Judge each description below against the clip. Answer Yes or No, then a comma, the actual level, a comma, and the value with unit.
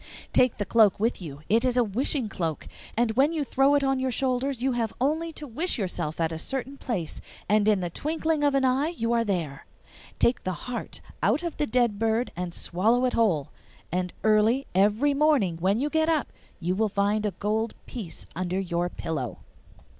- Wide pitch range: Yes, wide, 6.2 semitones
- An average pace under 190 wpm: No, average, 200 wpm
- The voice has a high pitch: Yes, high, 225 Hz